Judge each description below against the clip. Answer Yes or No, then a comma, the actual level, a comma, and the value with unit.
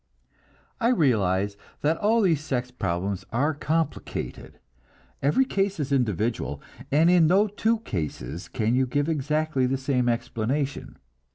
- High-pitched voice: No, medium, 140 Hz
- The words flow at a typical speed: No, slow, 130 wpm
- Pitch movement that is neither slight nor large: No, wide, 5.9 semitones